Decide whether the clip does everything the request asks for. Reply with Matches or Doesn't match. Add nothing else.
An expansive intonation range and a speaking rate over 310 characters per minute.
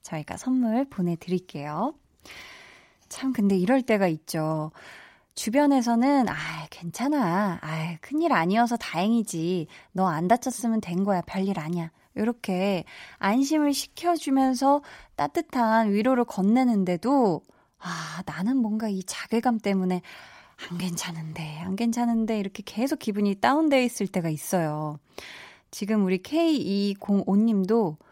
Doesn't match